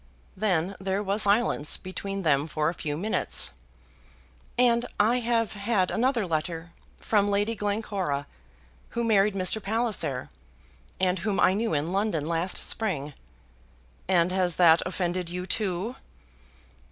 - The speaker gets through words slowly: Yes, slow, 130 wpm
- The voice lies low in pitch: No, high, 190 Hz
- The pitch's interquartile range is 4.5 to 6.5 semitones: No, average, 4.1 semitones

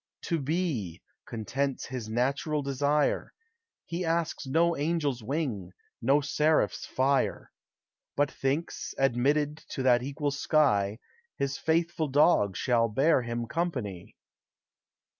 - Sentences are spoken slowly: Yes, slow, 110 wpm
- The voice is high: No, medium, 140 Hz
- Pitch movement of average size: Yes, average, 4.0 semitones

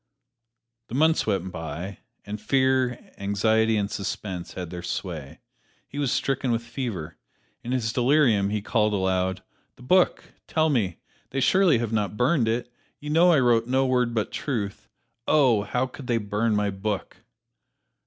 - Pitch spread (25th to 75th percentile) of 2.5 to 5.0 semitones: Yes, average, 4.5 semitones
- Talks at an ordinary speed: Yes, average, 160 wpm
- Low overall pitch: Yes, low, 115 Hz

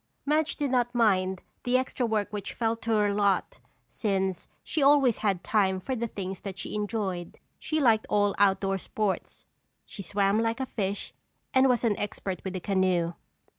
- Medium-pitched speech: No, high, 210 Hz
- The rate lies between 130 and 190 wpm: Yes, average, 170 wpm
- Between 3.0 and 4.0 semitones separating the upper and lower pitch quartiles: Yes, average, 3.7 semitones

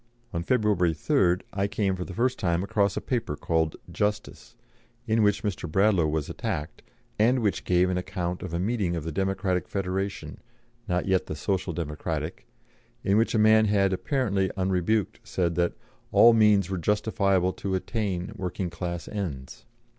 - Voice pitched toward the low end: Yes, very low, 95 Hz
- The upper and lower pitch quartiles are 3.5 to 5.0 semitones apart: No, average, 3.1 semitones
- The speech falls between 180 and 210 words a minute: No, average, 165 wpm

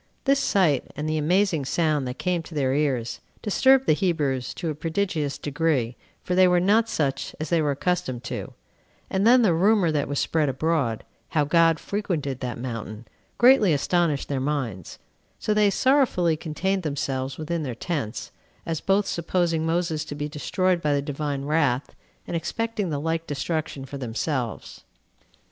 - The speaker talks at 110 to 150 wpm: No, average, 165 wpm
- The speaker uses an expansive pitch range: No, average, 4.3 semitones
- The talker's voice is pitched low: No, medium, 155 Hz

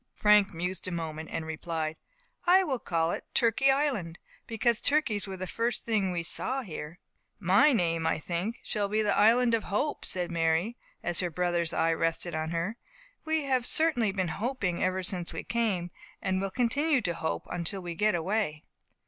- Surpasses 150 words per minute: Yes, average, 180 wpm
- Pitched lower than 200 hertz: Yes, high, 190 Hz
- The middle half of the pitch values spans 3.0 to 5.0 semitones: No, wide, 5.5 semitones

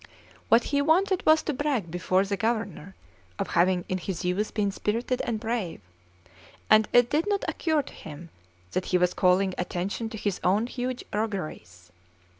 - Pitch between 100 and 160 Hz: No, high, 210 Hz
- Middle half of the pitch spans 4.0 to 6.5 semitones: Yes, average, 5.1 semitones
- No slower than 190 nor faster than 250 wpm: No, average, 170 wpm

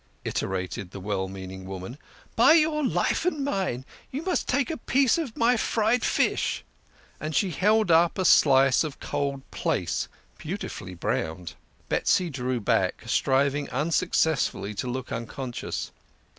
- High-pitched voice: No, medium, 140 Hz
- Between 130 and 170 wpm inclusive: Yes, average, 145 wpm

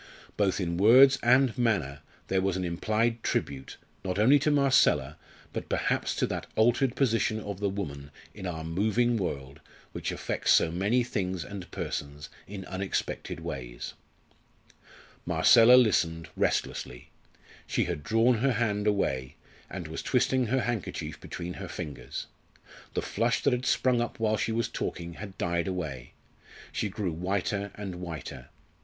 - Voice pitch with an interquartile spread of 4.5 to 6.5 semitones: Yes, wide, 5.5 semitones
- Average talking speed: Yes, average, 150 wpm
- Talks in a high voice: No, low, 100 Hz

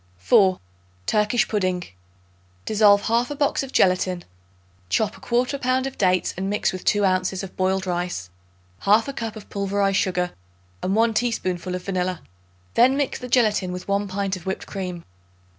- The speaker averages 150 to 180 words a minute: Yes, average, 160 wpm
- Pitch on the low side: No, high, 195 Hz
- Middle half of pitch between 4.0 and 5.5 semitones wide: No, average, 3.5 semitones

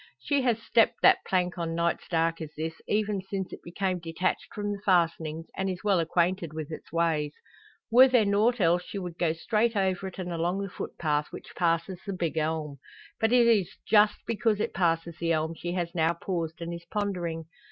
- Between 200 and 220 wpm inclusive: Yes, fast, 205 wpm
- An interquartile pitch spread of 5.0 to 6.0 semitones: No, average, 3.5 semitones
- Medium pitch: Yes, medium, 175 Hz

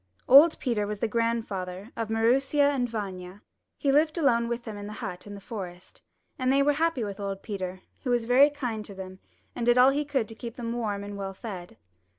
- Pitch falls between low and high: No, high, 230 Hz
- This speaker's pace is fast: Yes, fast, 220 wpm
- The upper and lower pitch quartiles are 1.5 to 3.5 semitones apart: No, average, 4.3 semitones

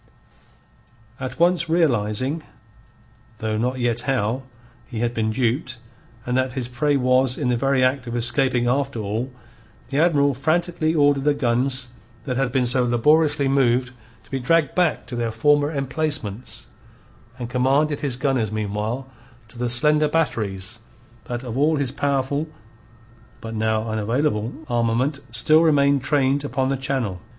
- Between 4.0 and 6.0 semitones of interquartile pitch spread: No, average, 3.3 semitones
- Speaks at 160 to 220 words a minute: No, average, 150 wpm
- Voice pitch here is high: No, low, 130 Hz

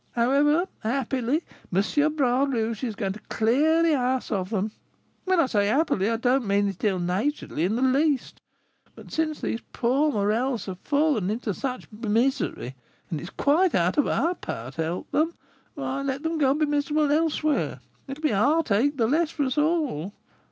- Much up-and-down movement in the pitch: Yes, wide, 5.8 semitones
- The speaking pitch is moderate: No, very high, 260 Hz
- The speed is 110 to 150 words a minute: No, average, 190 wpm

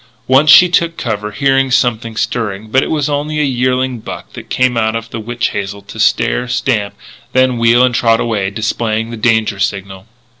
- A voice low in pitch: Yes, low, 115 Hz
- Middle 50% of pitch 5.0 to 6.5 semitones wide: No, average, 3.1 semitones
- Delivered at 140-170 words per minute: No, average, 190 wpm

